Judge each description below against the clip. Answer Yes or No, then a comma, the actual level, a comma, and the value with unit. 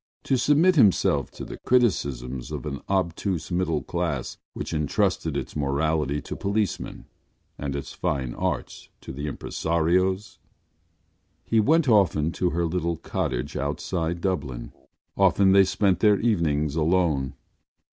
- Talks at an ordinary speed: No, slow, 125 wpm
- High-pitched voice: No, very low, 85 Hz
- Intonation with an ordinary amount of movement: Yes, average, 4.9 semitones